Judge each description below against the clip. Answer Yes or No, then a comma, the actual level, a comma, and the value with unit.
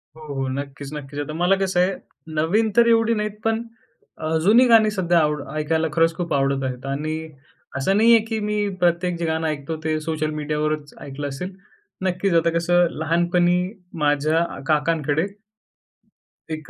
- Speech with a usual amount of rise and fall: Yes, average, 3.5 semitones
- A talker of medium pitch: Yes, medium, 160 Hz